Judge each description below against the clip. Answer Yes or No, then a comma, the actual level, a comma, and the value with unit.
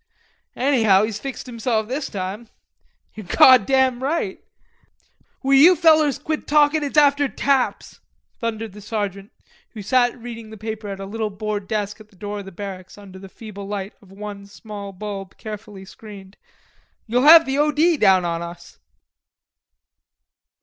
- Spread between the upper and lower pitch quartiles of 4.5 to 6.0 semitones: Yes, average, 4.9 semitones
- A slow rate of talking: No, average, 155 wpm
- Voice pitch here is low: No, high, 215 Hz